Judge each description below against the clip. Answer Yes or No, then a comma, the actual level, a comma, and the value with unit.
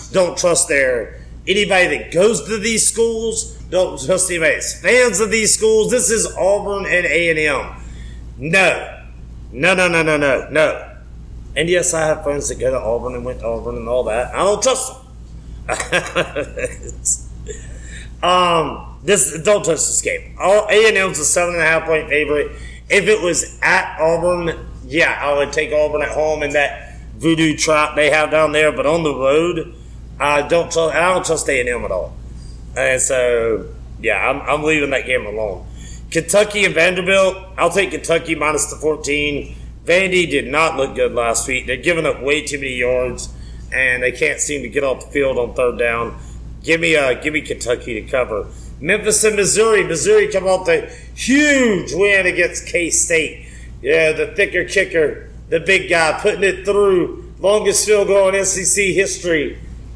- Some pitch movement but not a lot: No, wide, 7.1 semitones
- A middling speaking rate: Yes, average, 180 wpm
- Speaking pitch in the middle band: Yes, medium, 160 Hz